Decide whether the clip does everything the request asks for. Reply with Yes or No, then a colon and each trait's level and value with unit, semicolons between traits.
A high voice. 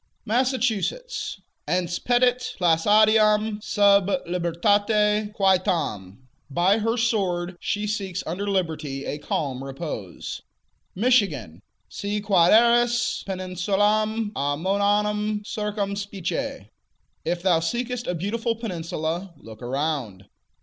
Yes: high, 200 Hz